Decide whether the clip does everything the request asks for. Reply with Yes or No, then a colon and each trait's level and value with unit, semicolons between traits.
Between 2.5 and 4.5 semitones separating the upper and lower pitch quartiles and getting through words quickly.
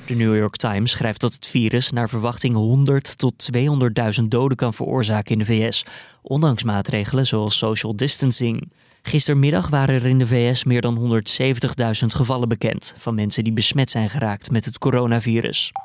No: average, 2.8 semitones; average, 165 wpm